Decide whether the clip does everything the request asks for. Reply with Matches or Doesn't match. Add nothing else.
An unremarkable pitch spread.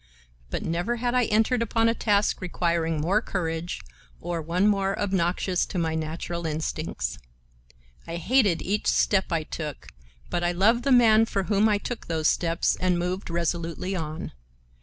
Matches